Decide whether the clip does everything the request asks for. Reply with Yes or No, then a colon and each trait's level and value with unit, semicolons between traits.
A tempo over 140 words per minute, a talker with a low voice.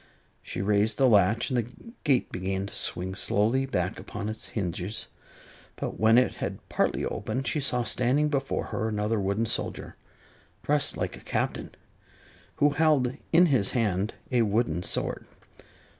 Yes: average, 155 wpm; low, 115 Hz